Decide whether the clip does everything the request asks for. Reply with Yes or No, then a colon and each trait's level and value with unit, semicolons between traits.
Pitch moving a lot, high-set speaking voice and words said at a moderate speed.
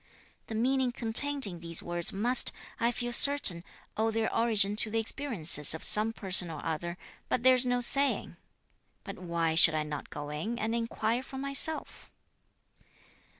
Yes: wide, 6.3 semitones; high, 220 Hz; average, 160 wpm